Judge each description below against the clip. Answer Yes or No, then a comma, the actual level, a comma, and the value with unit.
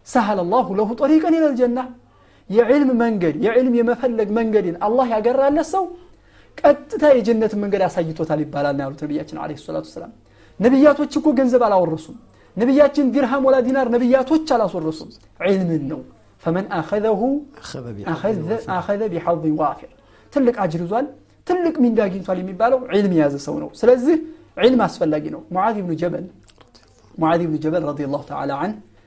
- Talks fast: Yes, fast, 160 wpm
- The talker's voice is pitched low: No, high, 220 Hz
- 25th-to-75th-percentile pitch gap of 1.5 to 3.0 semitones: No, wide, 7.6 semitones